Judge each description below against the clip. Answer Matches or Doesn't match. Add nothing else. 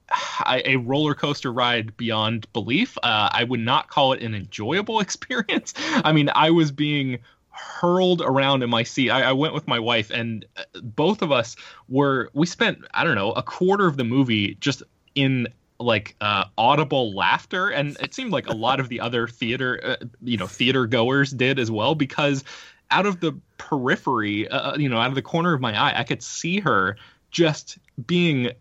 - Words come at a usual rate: Matches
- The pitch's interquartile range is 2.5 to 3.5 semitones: Doesn't match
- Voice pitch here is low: Matches